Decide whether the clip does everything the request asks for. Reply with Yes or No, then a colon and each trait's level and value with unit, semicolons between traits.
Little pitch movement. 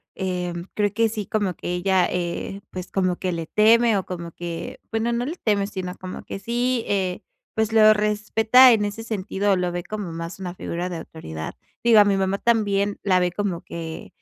No: average, 3.2 semitones